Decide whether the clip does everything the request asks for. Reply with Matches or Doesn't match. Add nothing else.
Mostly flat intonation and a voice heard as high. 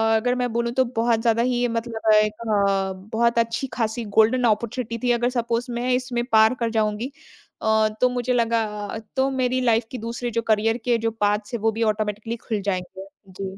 Matches